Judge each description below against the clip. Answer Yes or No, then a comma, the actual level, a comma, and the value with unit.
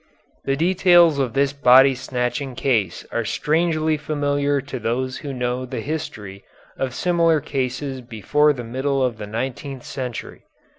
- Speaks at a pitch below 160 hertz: Yes, low, 135 Hz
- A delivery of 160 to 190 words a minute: No, average, 145 wpm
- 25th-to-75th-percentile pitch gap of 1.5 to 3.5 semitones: Yes, average, 2.9 semitones